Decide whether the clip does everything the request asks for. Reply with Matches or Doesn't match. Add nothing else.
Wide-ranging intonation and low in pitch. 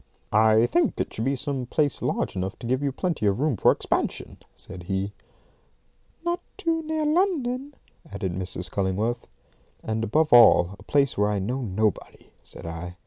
Matches